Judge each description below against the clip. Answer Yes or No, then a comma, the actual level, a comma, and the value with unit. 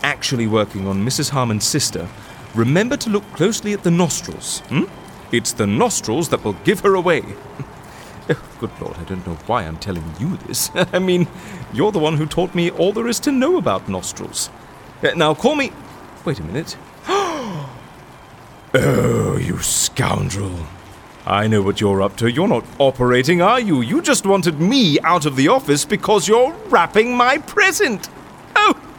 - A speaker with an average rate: Yes, average, 165 wpm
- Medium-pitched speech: Yes, medium, 155 Hz